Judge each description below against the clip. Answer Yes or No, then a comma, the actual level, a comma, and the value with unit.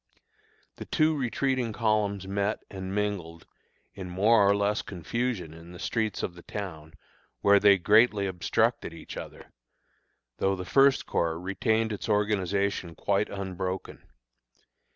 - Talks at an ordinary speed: No, slow, 130 wpm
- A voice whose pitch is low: Yes, low, 100 Hz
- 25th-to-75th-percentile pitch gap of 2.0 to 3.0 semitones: Yes, average, 2.7 semitones